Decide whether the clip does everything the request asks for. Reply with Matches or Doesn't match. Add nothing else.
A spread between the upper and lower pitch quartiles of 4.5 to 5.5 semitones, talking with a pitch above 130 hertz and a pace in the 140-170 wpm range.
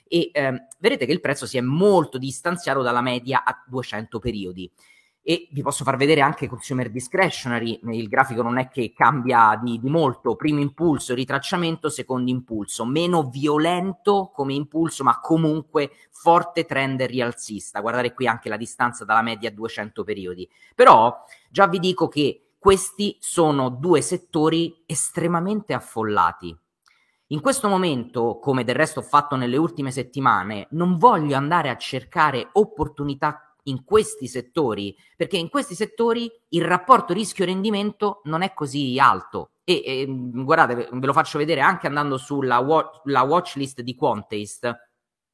Matches